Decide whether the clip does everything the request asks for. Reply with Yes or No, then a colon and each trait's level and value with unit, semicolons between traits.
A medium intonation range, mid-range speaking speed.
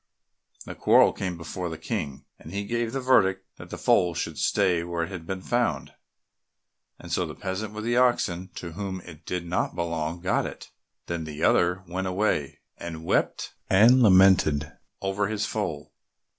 Yes: average, 3.3 semitones; average, 175 wpm